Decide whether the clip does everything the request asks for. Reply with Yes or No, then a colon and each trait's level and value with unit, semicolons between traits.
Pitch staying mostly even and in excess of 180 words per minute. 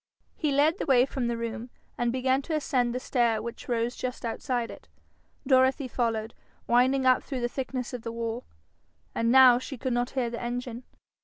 Yes: narrow, 1.8 semitones; average, 190 wpm